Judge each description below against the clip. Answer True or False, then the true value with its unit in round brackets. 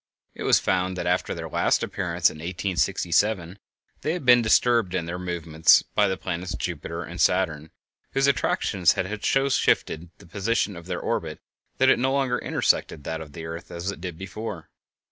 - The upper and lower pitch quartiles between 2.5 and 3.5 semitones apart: False (4.1 semitones)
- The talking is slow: False (185 wpm)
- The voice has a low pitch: True (90 Hz)